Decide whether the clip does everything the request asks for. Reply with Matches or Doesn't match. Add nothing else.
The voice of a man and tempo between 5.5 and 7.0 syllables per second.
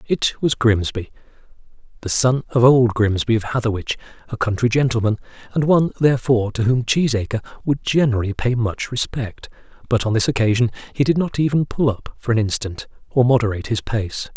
Matches